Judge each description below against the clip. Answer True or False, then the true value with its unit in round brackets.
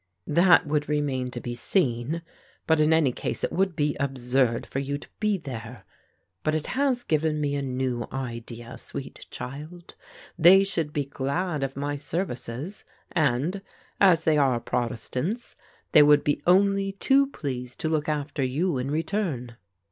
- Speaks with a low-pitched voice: False (145 Hz)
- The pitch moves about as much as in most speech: True (4.6 semitones)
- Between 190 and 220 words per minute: False (160 wpm)